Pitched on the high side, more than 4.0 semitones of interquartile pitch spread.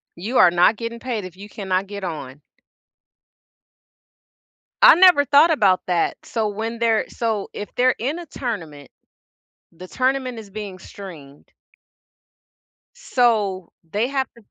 Yes: high, 215 Hz; wide, 5.4 semitones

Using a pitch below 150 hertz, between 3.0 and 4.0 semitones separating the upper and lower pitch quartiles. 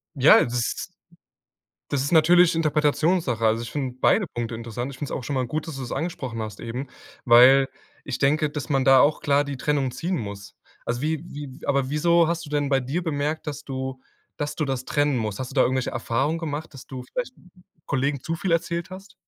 Yes: medium, 140 Hz; average, 3.5 semitones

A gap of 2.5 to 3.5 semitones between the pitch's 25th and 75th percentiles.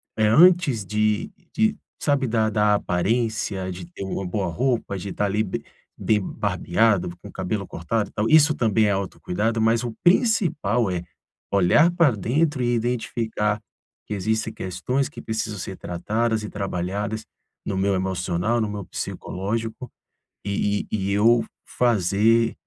Yes: average, 3.2 semitones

